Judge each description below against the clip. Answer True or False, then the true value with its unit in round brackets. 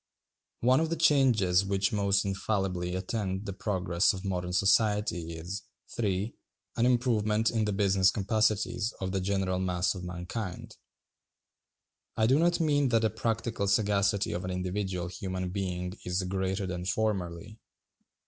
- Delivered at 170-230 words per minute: False (145 wpm)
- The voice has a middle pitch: False (100 Hz)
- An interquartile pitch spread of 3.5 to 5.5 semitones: False (3.1 semitones)